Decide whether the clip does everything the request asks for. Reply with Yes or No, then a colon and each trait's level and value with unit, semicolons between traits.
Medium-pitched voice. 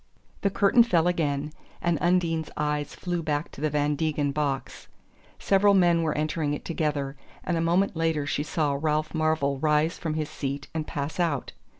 Yes: medium, 155 Hz